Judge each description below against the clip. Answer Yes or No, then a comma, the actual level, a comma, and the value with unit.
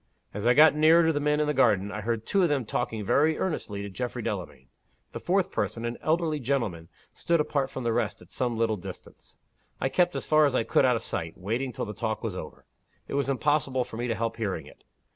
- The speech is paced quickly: Yes, fast, 240 wpm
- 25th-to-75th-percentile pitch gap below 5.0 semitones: No, average, 5.3 semitones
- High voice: No, low, 125 Hz